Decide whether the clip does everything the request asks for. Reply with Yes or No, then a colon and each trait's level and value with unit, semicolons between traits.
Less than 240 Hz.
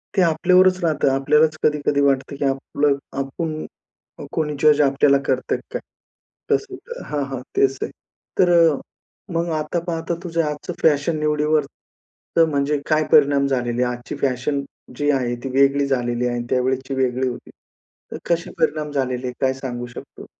Yes: medium, 140 Hz